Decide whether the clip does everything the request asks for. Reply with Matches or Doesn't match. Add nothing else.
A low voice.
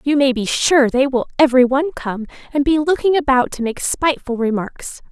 Doesn't match